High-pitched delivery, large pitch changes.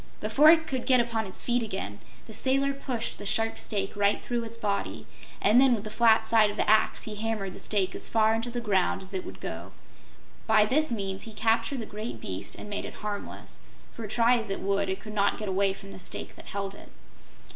No: high, 215 Hz; average, 2.7 semitones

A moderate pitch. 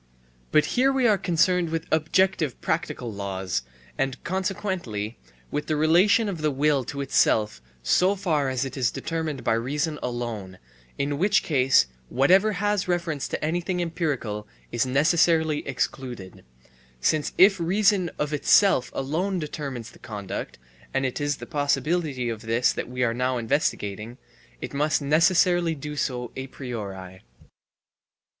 Yes: medium, 150 Hz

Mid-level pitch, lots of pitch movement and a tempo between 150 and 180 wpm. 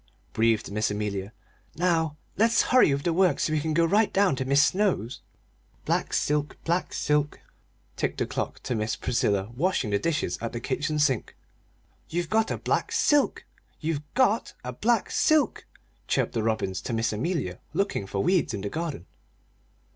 Yes: medium, 150 Hz; wide, 8.1 semitones; average, 170 wpm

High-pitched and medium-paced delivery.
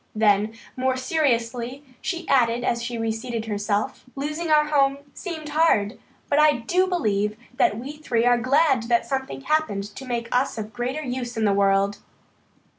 Yes: high, 245 Hz; average, 165 wpm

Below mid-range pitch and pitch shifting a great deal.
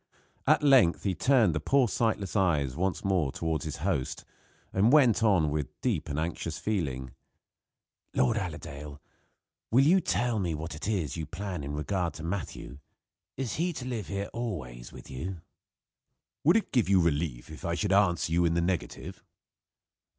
Yes: very low, 90 Hz; wide, 5.9 semitones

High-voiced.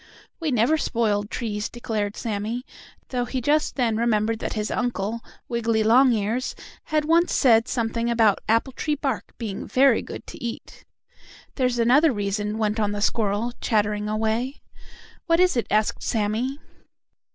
Yes: high, 230 Hz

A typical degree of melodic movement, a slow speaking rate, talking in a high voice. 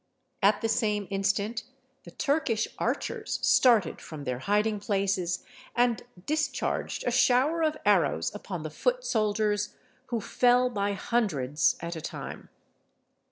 Yes: average, 3.9 semitones; slow, 130 wpm; high, 215 Hz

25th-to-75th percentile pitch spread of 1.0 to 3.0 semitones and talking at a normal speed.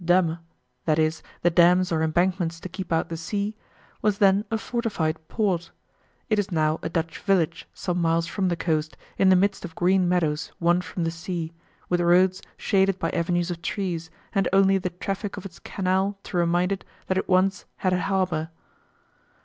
Yes: narrow, 2.5 semitones; average, 185 wpm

